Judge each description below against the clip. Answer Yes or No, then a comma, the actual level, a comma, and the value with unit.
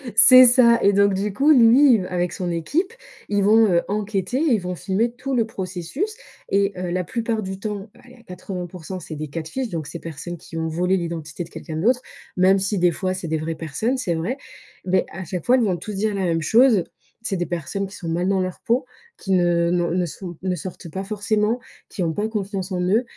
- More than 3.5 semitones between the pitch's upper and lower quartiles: Yes, average, 4.2 semitones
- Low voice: No, high, 190 Hz